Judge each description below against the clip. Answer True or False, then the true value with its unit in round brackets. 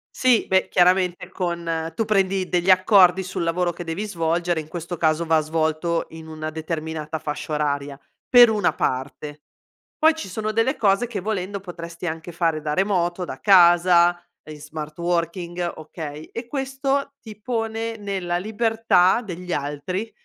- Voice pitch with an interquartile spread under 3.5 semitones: False (3.9 semitones)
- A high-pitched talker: False (175 Hz)